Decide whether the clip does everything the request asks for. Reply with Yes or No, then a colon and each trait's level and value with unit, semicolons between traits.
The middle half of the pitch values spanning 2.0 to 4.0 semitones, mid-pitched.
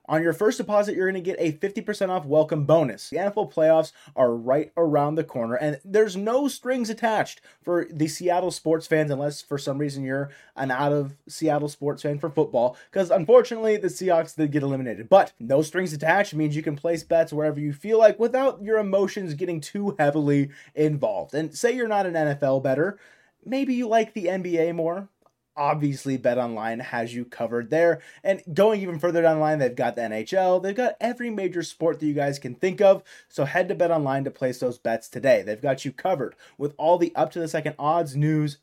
No: average, 4.9 semitones; medium, 160 Hz